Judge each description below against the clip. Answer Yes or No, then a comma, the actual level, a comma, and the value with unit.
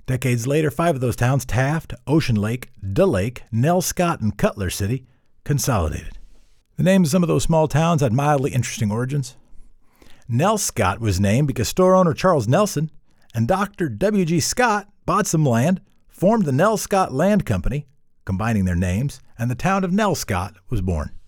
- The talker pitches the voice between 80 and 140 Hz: Yes, low, 135 Hz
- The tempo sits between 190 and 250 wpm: No, average, 175 wpm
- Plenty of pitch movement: Yes, wide, 7.3 semitones